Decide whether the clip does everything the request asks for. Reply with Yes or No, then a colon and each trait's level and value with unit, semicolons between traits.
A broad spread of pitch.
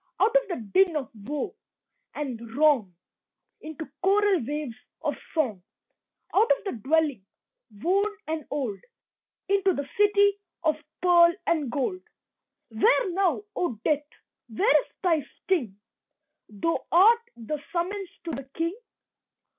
Yes: wide, 6.4 semitones